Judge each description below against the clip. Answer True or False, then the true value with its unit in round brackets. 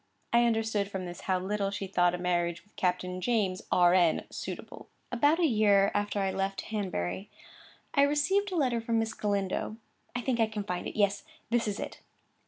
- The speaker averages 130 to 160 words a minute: False (185 wpm)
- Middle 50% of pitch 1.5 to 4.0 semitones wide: True (3.6 semitones)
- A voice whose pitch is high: True (205 Hz)